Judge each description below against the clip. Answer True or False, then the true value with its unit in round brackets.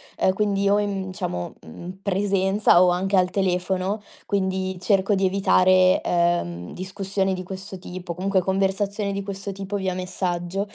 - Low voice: False (190 Hz)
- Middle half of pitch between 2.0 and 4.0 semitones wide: False (1.3 semitones)